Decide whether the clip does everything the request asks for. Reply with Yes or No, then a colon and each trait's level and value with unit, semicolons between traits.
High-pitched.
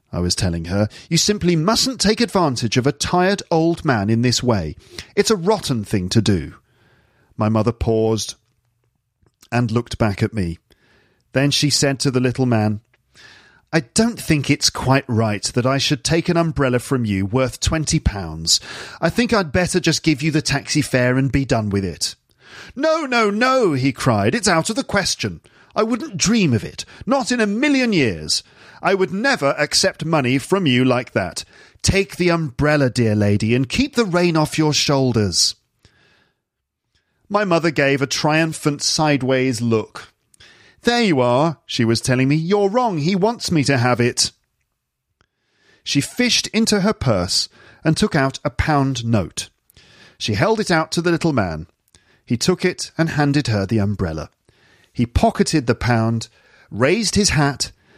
No: medium, 140 Hz